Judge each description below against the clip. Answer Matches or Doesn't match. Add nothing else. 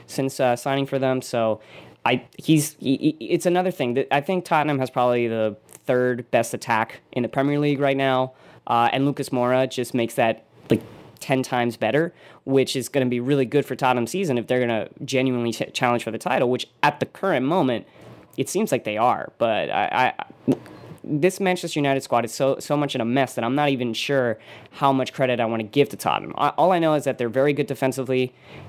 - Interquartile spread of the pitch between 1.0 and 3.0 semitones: Matches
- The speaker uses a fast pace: Matches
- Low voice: Matches